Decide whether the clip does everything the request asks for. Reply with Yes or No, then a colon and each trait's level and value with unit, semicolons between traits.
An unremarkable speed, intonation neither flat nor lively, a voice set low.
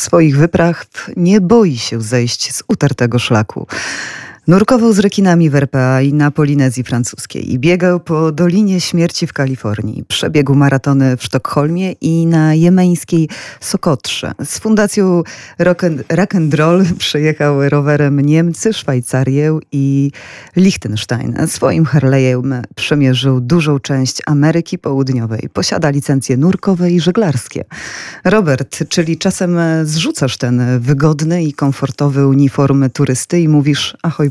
No: average, 120 wpm; average, 4.3 semitones; medium, 150 Hz